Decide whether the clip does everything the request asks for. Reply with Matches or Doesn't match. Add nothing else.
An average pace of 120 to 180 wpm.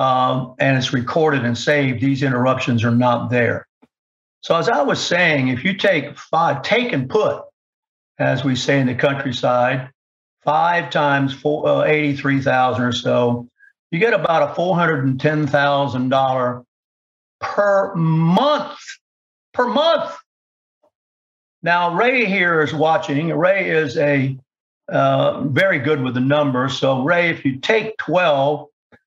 Matches